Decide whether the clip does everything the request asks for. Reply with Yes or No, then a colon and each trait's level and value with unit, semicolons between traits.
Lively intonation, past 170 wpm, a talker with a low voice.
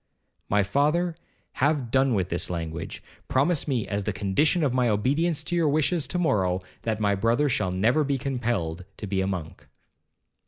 Yes: wide, 7.2 semitones; average, 180 wpm; low, 120 Hz